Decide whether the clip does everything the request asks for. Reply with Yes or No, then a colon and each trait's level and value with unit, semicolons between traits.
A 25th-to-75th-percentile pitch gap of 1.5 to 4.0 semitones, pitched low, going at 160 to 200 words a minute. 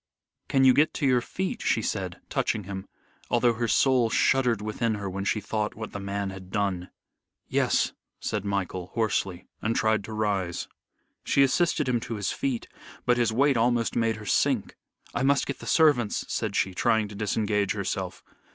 Yes: average, 3.5 semitones; low, 110 Hz; average, 180 wpm